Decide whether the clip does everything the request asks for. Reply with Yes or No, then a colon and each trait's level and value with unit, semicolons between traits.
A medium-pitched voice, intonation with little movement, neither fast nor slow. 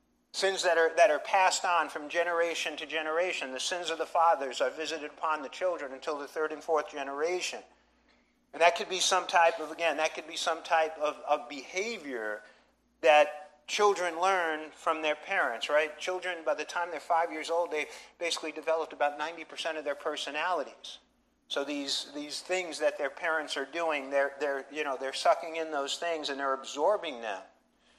Yes: medium, 160 Hz; narrow, 2.3 semitones; average, 190 wpm